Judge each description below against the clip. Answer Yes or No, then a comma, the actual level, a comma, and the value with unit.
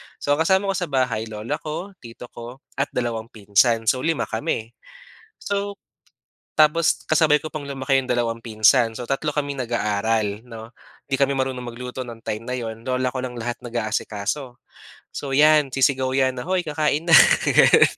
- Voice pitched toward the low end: Yes, low, 130 Hz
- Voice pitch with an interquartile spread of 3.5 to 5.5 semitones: Yes, average, 4.2 semitones